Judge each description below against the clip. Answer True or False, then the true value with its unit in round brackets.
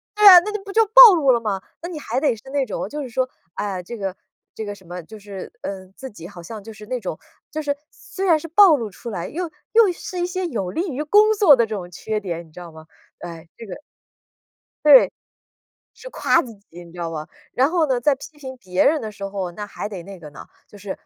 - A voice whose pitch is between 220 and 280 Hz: True (230 Hz)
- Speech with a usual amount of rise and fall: False (8.3 semitones)